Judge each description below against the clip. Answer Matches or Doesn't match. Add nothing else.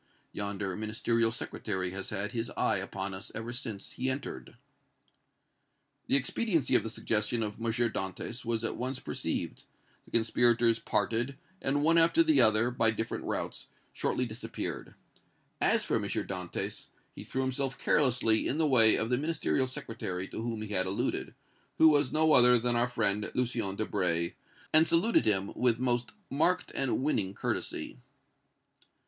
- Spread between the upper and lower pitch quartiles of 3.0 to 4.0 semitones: Matches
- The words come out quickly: Doesn't match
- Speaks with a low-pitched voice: Matches